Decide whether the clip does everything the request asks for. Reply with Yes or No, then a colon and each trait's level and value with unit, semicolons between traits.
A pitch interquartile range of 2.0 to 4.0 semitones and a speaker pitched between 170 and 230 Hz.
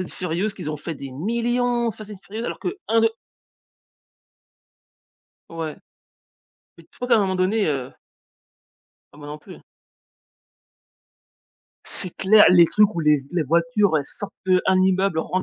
No: average, 5.0 semitones; medium, 185 Hz